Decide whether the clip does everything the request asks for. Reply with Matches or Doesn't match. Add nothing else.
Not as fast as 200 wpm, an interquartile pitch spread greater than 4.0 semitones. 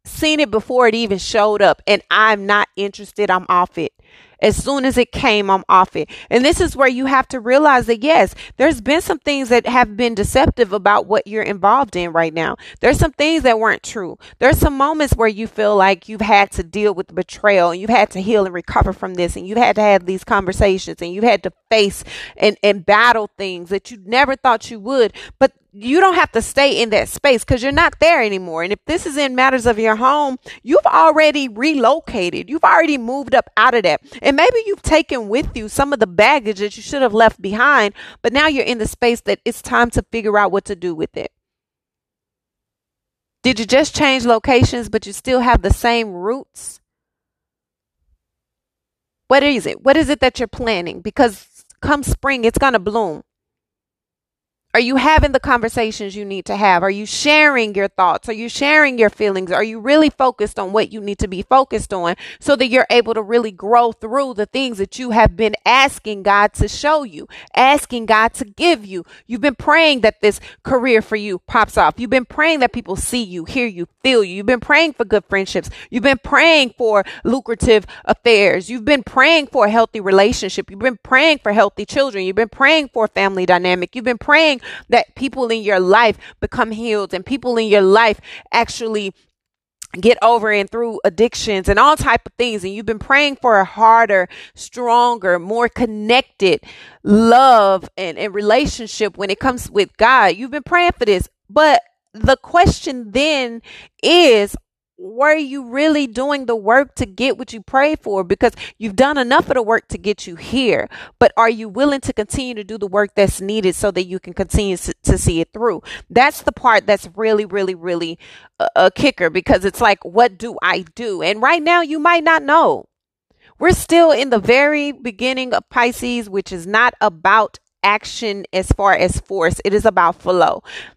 Doesn't match